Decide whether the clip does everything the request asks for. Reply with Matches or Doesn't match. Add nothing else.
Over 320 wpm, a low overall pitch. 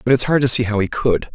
Matches